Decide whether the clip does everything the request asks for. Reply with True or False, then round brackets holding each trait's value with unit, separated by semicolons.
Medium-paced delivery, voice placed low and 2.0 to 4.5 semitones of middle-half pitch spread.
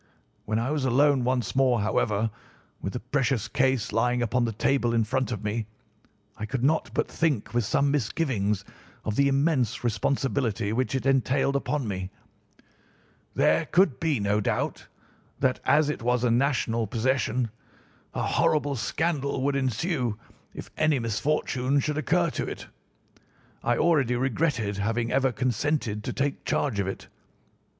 True (155 wpm; 125 Hz; 3.6 semitones)